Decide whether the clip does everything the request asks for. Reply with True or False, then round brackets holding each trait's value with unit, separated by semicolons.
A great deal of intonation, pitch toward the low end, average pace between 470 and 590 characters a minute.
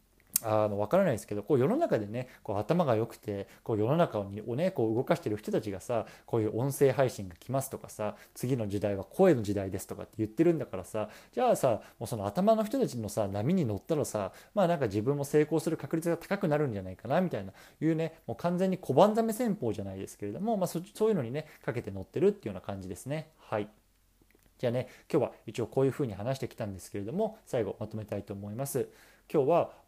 True (7.5 semitones; 120 Hz; 475 characters per minute)